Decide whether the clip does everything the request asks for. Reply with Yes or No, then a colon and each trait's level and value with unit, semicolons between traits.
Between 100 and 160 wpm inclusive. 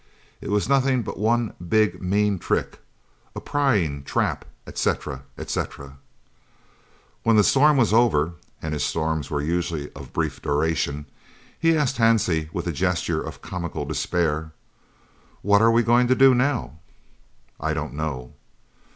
Yes: average, 140 wpm